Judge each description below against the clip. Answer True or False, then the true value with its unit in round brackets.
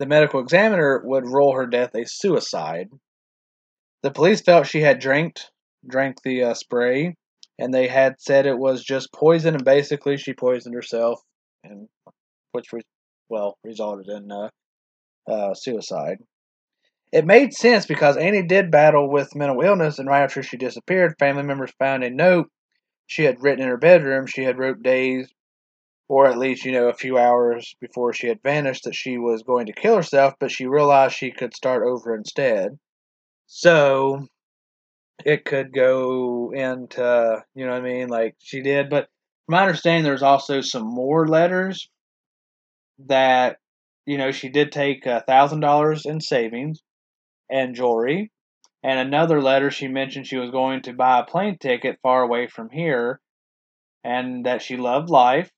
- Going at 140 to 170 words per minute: True (165 wpm)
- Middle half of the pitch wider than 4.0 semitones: False (2.7 semitones)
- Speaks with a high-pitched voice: False (135 Hz)